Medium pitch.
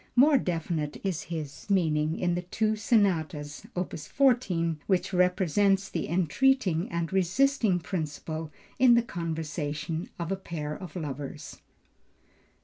Yes: medium, 175 Hz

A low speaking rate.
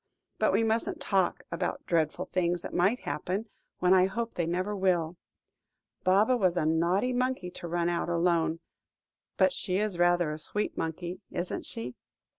No: average, 165 wpm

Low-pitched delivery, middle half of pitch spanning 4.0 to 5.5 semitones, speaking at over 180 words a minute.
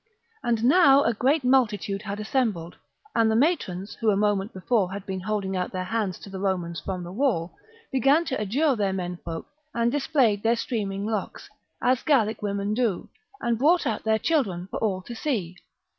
No: high, 215 Hz; average, 4.7 semitones; average, 190 wpm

